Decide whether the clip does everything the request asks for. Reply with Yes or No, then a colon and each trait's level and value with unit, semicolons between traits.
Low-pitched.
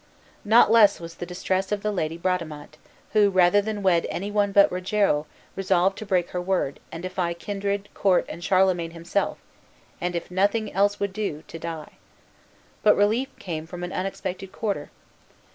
No: medium, 185 Hz